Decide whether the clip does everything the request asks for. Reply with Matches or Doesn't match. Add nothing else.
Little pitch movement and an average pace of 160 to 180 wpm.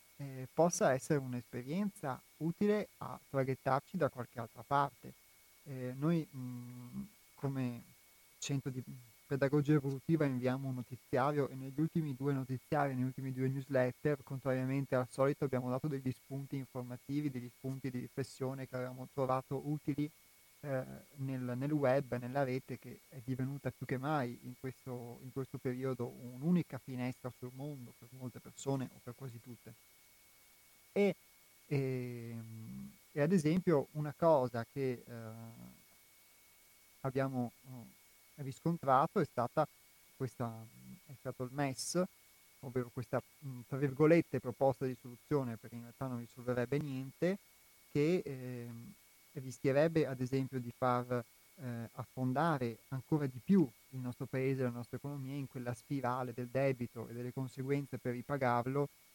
Doesn't match